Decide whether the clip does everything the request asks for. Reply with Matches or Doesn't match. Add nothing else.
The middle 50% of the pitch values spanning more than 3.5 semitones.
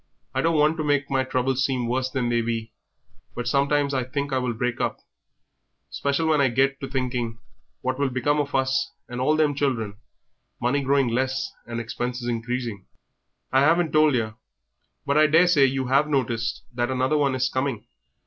Doesn't match